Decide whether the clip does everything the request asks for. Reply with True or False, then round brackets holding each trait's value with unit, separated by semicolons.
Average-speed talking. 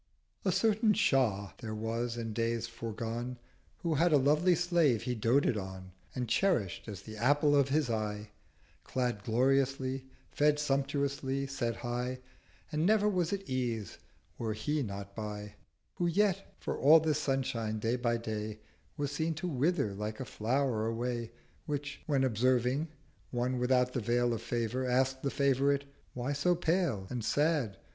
True (155 wpm)